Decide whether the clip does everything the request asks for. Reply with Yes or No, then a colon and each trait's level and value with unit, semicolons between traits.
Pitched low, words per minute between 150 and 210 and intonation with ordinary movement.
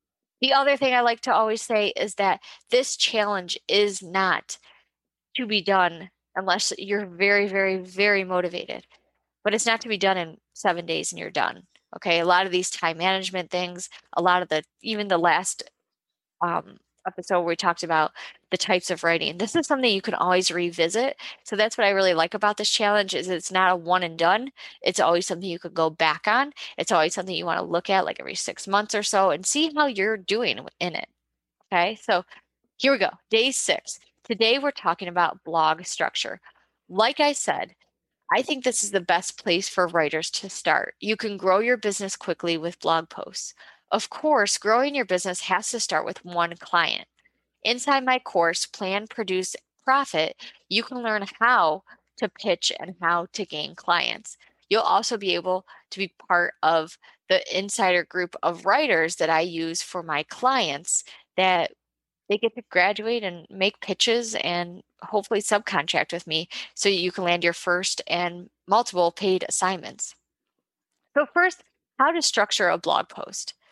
No: high, 190 Hz; average, 185 wpm; average, 3.9 semitones